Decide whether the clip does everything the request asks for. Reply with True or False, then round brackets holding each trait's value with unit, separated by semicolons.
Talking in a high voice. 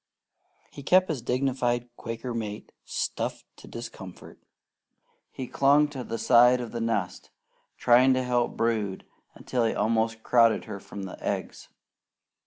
False (120 Hz)